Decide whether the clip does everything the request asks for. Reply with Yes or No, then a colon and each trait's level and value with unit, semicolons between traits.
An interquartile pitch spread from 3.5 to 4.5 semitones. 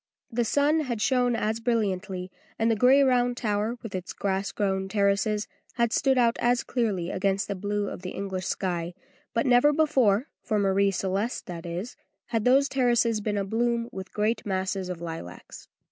Yes: average, 4.0 semitones